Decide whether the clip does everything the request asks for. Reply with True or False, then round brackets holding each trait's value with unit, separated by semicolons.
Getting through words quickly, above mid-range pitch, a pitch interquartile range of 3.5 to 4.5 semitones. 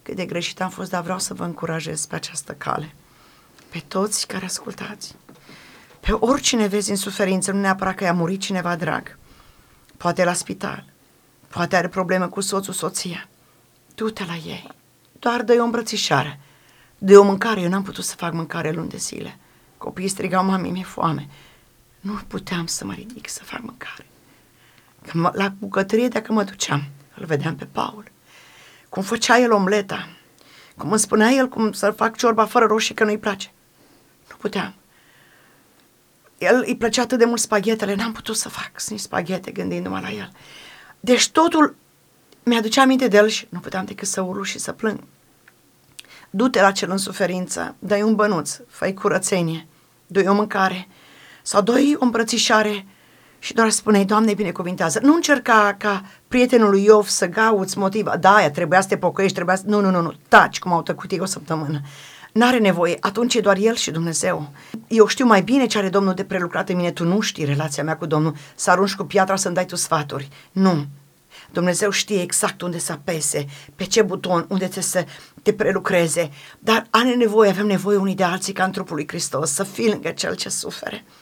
True (180 wpm; 195 Hz; 3.8 semitones)